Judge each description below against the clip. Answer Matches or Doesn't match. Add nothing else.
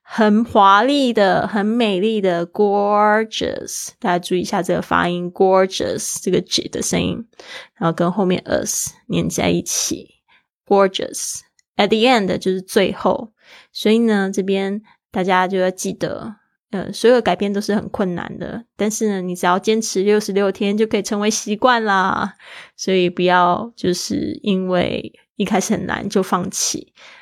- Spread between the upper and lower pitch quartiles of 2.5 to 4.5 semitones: Matches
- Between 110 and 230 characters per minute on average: Doesn't match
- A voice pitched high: Matches